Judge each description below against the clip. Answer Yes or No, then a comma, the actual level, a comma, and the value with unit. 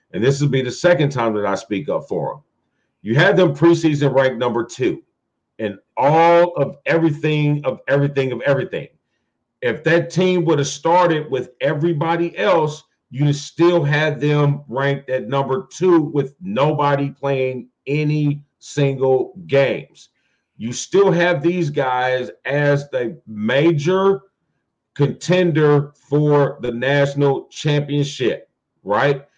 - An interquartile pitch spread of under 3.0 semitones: No, average, 3.5 semitones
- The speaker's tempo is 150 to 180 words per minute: No, slow, 135 wpm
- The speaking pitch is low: No, medium, 145 Hz